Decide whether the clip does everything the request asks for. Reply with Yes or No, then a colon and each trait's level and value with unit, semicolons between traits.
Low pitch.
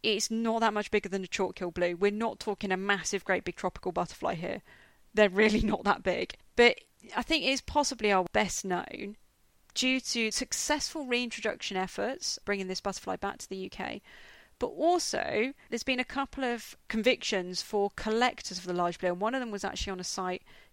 No: high, 210 Hz